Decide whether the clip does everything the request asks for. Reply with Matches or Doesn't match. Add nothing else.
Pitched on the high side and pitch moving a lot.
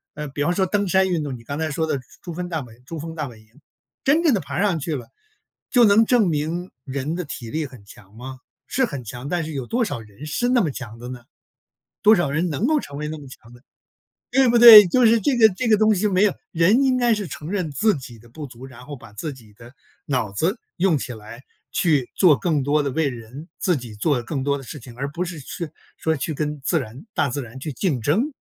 Doesn't match